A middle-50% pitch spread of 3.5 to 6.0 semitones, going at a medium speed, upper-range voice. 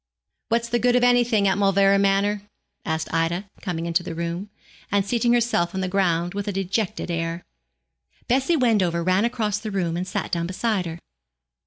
Yes: average, 4.3 semitones; average, 180 wpm; high, 195 Hz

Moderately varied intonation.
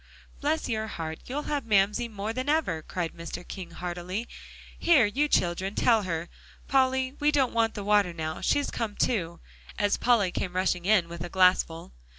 No: wide, 5.9 semitones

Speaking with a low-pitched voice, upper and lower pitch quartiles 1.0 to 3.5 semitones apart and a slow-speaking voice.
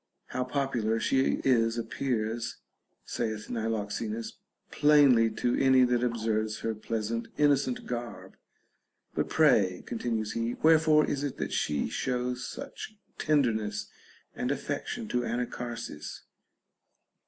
Yes: low, 120 Hz; average, 2.9 semitones; slow, 115 wpm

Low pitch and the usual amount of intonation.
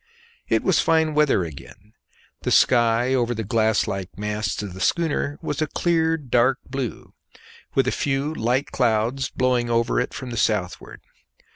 Yes: low, 120 Hz; average, 4.2 semitones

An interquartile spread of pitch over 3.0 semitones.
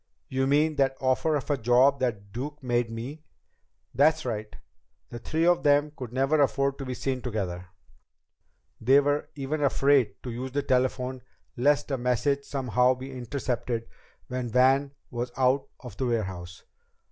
No: narrow, 2.6 semitones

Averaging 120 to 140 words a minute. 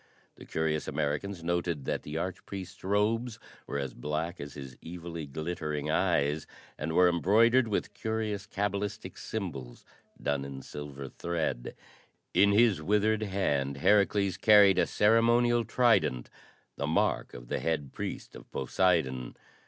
Yes: slow, 135 wpm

